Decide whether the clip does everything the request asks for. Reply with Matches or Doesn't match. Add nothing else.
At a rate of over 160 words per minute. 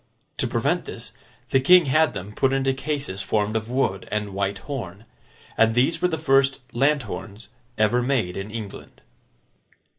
Doesn't match